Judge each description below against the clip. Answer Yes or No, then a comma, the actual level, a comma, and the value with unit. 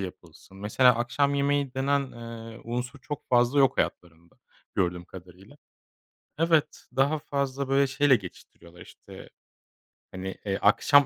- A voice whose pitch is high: No, low, 125 Hz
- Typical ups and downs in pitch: No, wide, 6.3 semitones